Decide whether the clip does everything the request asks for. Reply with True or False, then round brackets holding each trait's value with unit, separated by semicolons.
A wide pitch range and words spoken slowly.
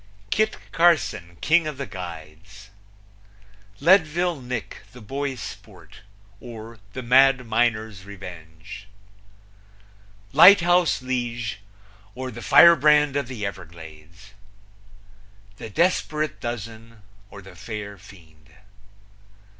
True (6.5 semitones; 95 wpm)